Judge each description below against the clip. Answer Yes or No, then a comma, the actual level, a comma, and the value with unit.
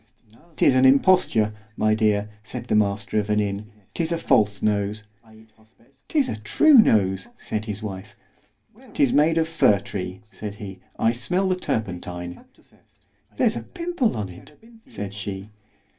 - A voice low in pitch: Yes, low, 105 Hz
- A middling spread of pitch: Yes, average, 4.7 semitones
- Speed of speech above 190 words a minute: No, average, 145 wpm